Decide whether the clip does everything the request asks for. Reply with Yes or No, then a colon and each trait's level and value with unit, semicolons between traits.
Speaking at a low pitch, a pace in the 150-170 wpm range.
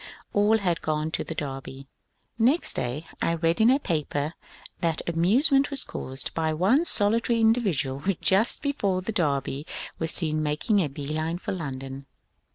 No: medium, 165 Hz; average, 165 wpm